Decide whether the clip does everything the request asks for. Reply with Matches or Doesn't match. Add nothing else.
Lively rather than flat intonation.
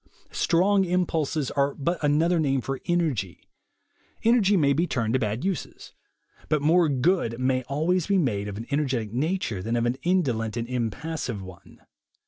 Matches